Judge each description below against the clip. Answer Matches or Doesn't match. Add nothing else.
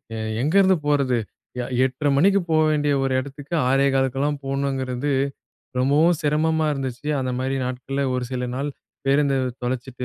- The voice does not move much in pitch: Matches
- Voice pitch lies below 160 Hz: Matches